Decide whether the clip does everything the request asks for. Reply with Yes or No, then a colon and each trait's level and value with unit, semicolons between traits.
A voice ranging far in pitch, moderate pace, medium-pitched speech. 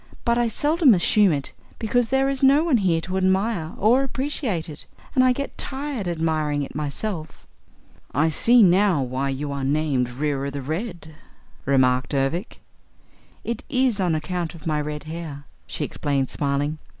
Yes: wide, 8.1 semitones; average, 160 wpm; medium, 165 Hz